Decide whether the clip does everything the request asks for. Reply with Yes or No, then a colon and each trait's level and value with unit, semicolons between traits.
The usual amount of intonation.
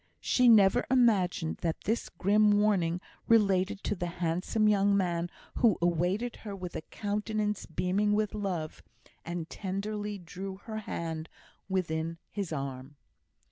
Yes: average, 3.5 semitones